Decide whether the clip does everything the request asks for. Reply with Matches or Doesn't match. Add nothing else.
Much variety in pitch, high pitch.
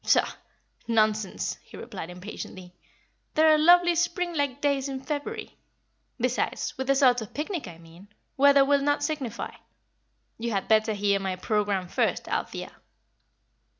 Matches